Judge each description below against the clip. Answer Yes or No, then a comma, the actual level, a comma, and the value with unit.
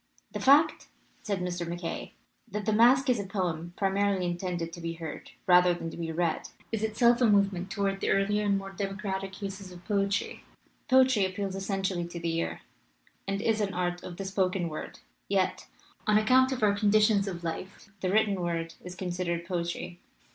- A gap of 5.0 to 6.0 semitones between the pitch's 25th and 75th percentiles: No, average, 2.8 semitones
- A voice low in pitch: No, high, 195 Hz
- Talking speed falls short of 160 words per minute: No, average, 190 wpm